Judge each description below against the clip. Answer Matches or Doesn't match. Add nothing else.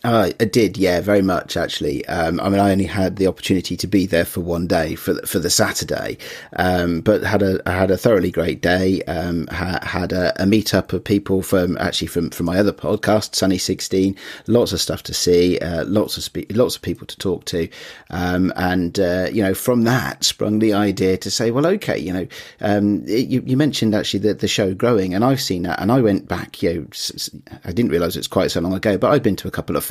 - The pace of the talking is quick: Matches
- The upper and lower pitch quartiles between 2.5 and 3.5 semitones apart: Matches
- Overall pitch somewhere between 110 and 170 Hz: Doesn't match